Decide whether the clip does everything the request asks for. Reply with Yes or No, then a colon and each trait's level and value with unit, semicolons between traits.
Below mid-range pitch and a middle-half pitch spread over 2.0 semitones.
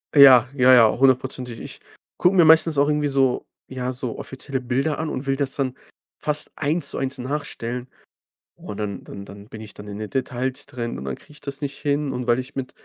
Yes: low, 130 Hz; narrow, 2.6 semitones